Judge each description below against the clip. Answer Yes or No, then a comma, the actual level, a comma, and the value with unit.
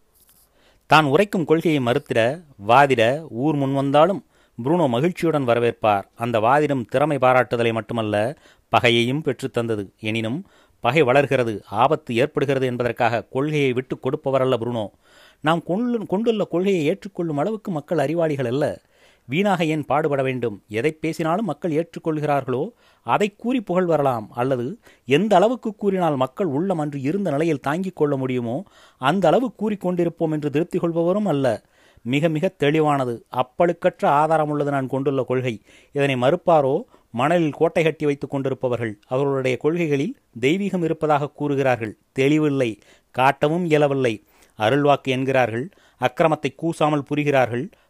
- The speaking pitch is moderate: Yes, medium, 145 Hz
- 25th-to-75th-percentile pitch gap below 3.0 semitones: No, average, 4.4 semitones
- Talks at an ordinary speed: Yes, average, 120 wpm